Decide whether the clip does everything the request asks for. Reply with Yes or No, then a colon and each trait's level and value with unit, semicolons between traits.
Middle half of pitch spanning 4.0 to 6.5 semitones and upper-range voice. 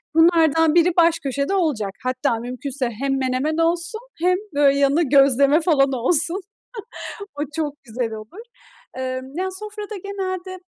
Yes: average, 4.9 semitones; very high, 295 Hz